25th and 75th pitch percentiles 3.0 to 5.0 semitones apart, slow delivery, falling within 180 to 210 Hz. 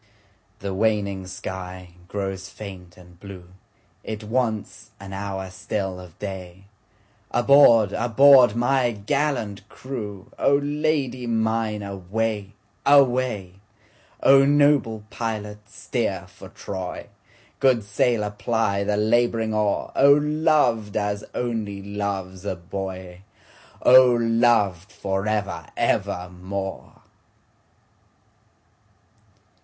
No: average, 3.5 semitones; slow, 85 wpm; low, 105 Hz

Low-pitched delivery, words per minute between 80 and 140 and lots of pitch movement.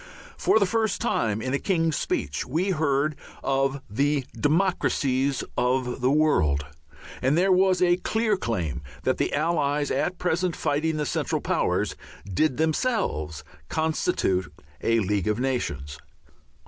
No: medium, 145 Hz; slow, 135 wpm; wide, 6.3 semitones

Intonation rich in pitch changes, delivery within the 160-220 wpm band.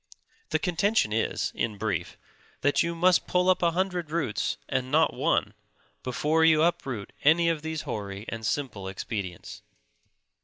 No: wide, 7.6 semitones; average, 150 wpm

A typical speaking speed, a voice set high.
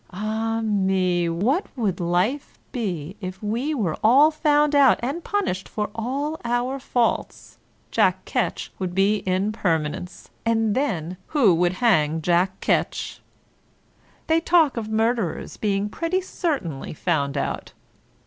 No: slow, 130 wpm; high, 215 Hz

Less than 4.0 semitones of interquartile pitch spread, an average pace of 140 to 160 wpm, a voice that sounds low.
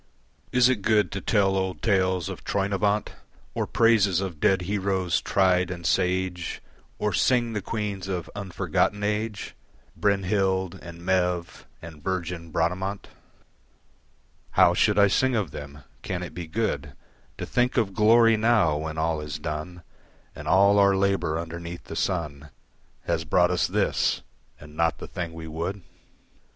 Yes: average, 3.2 semitones; average, 150 wpm; very low, 95 Hz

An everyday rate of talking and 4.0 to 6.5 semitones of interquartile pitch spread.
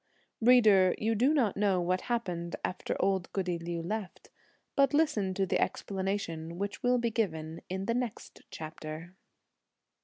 Yes: average, 150 wpm; average, 4.7 semitones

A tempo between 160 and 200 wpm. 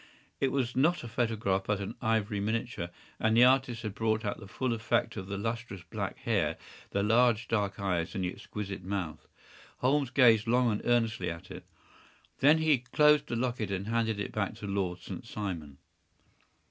Yes: average, 185 wpm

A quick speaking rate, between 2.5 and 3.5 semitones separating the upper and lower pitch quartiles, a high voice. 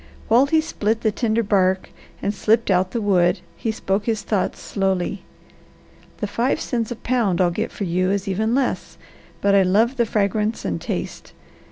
No: average, 180 wpm; average, 3.2 semitones; high, 210 Hz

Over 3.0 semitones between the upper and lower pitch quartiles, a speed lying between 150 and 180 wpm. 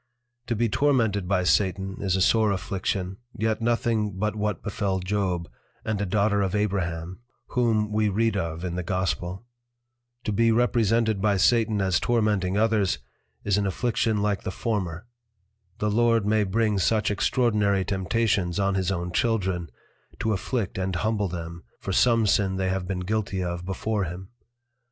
No: average, 2.7 semitones; average, 160 wpm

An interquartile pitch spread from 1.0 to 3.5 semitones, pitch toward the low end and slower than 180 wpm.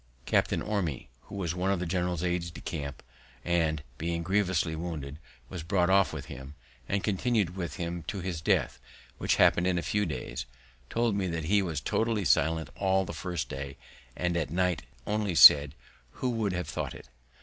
No: average, 3.2 semitones; very low, 90 Hz; average, 185 wpm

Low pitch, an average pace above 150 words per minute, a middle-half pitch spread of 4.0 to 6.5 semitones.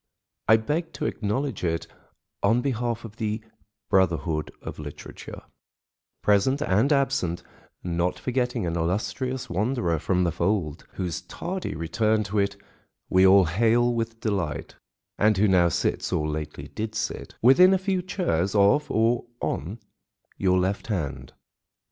No: low, 105 Hz; slow, 135 wpm; average, 5.3 semitones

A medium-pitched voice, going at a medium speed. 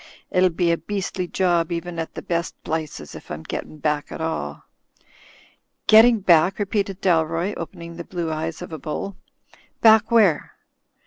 Yes: medium, 170 Hz; average, 155 wpm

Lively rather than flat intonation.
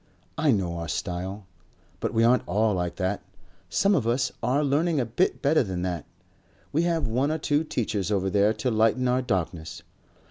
Yes: wide, 6.5 semitones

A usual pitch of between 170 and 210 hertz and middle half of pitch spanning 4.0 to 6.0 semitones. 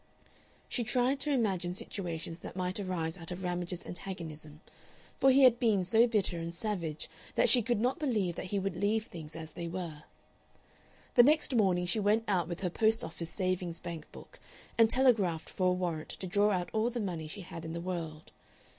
Yes: medium, 185 Hz; average, 4.6 semitones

